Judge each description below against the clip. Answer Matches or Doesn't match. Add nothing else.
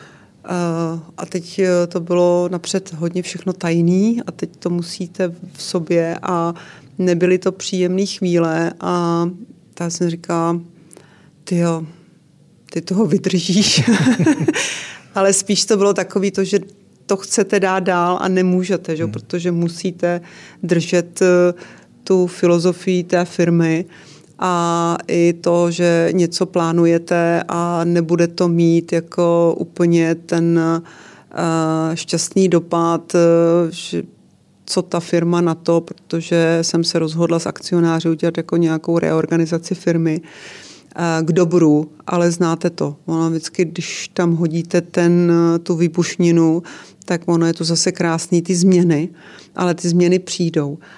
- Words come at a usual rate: Matches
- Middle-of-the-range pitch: Matches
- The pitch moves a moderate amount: Doesn't match